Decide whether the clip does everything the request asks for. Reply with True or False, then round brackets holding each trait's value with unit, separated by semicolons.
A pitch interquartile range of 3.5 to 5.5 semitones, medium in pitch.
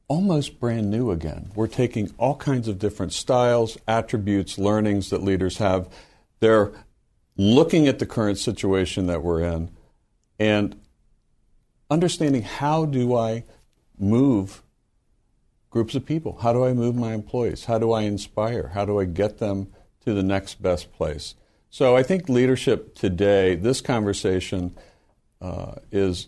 False (3.9 semitones; 110 Hz)